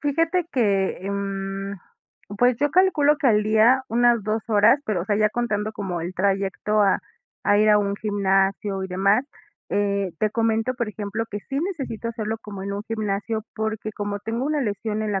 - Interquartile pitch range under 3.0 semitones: Yes, narrow, 2.6 semitones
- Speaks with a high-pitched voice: Yes, high, 215 Hz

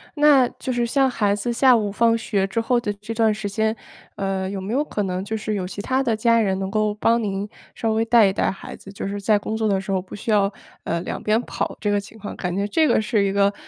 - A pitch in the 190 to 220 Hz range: Yes, high, 210 Hz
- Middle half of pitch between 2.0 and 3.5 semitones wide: Yes, narrow, 2.5 semitones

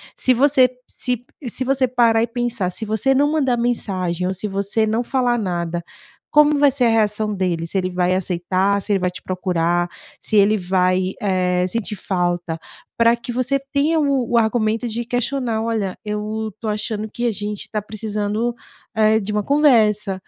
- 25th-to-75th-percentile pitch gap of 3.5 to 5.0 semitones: Yes, average, 4.3 semitones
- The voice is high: Yes, high, 215 Hz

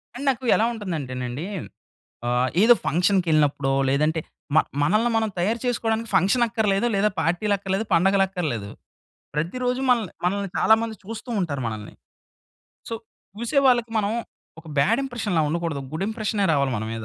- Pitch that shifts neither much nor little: No, wide, 6.5 semitones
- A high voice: Yes, high, 195 Hz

